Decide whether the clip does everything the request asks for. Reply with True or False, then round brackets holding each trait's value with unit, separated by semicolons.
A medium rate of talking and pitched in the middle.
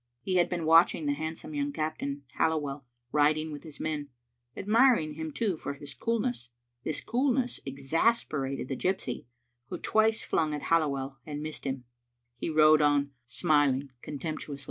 True (155 wpm; 155 Hz)